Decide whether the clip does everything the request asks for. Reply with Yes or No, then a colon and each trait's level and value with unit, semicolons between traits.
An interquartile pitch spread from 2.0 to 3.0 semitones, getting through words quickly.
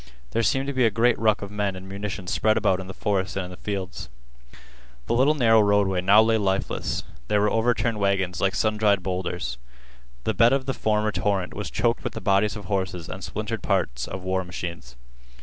Yes: average, 2.7 semitones; fast, 210 wpm